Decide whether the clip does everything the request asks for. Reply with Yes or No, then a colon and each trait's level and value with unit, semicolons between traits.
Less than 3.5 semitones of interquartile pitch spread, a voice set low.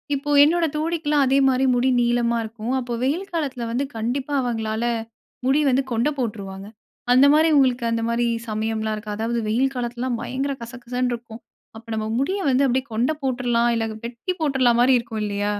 No: average, 2.8 semitones; high, 245 Hz